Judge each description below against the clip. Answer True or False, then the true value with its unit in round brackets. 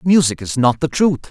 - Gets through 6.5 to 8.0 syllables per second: False (5.4 syllables/s)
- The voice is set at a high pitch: False (140 Hz)